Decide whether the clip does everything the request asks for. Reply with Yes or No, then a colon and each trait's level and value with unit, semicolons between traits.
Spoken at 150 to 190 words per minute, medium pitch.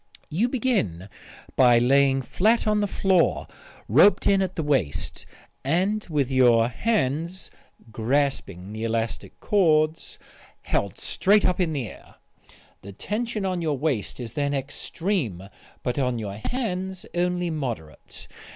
No: slow, 135 wpm; medium, 150 Hz